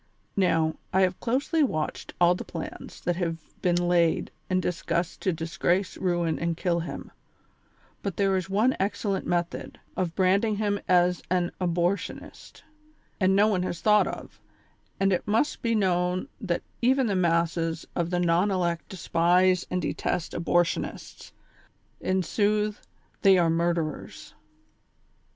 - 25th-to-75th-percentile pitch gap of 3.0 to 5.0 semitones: No, narrow, 2.4 semitones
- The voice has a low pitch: No, medium, 180 Hz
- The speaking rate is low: No, average, 145 wpm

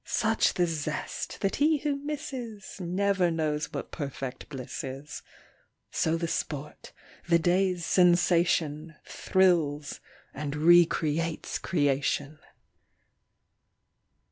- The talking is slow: Yes, slow, 95 wpm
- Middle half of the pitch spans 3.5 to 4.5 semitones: Yes, average, 4.0 semitones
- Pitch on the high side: No, medium, 170 Hz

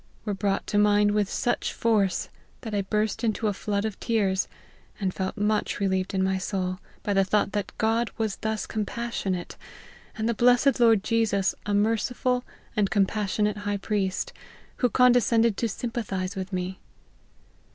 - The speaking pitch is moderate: No, high, 210 Hz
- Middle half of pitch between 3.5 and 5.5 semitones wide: No, narrow, 2.6 semitones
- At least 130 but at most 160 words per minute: No, average, 170 wpm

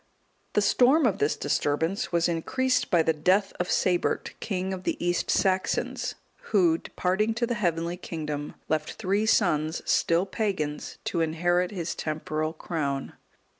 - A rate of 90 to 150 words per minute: Yes, average, 145 wpm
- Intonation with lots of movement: No, average, 3.9 semitones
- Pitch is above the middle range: No, medium, 175 Hz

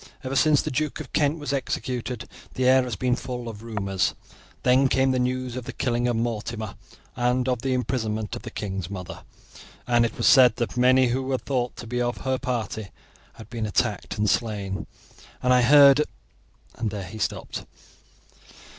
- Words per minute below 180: No, average, 185 wpm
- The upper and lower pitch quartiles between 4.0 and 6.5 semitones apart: No, average, 2.7 semitones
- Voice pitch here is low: Yes, low, 125 Hz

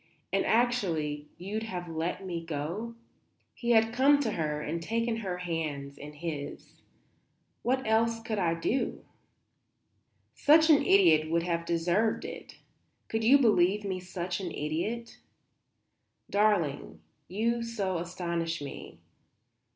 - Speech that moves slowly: Yes, slow, 130 wpm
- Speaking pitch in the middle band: Yes, medium, 180 Hz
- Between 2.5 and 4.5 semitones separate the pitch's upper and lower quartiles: No, average, 5.3 semitones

